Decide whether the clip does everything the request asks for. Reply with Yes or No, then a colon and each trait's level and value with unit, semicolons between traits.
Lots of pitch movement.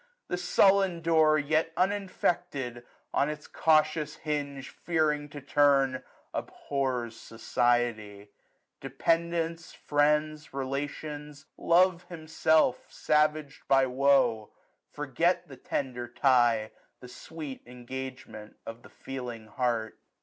No: average, 4.0 semitones